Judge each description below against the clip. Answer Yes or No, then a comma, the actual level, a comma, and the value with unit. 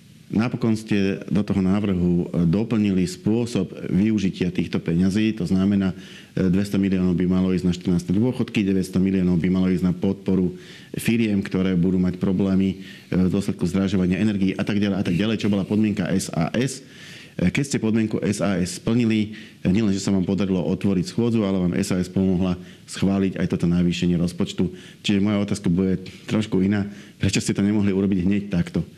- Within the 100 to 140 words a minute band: No, fast, 165 wpm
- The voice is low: Yes, very low, 95 Hz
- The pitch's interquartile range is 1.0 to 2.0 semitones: No, narrow, 2.5 semitones